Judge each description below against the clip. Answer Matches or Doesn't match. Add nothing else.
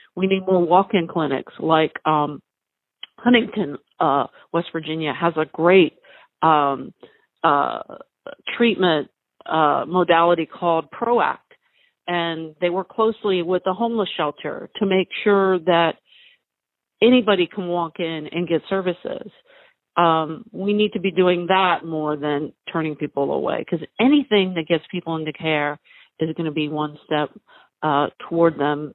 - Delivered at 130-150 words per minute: Matches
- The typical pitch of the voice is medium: Matches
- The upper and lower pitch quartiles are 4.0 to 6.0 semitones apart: Matches